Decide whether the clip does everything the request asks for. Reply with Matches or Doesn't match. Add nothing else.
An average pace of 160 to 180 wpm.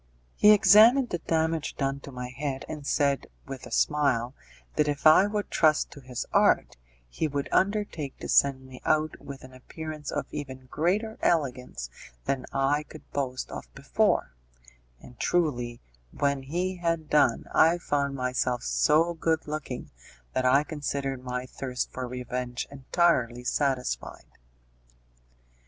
Doesn't match